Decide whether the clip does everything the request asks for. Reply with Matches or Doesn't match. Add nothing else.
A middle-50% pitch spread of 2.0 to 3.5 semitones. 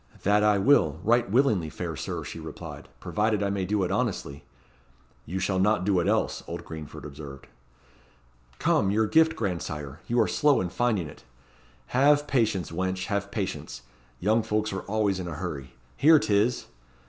Doesn't match